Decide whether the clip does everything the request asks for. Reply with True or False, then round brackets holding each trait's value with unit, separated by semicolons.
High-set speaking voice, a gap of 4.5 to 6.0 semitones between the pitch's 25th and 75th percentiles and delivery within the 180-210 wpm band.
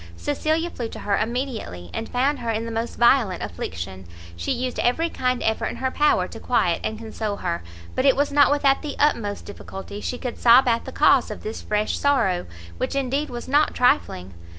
True (240 Hz; 4.9 semitones; 200 wpm)